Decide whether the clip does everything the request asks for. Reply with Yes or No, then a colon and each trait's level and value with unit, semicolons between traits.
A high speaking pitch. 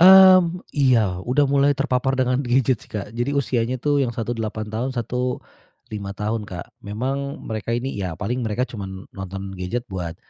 No: low, 120 Hz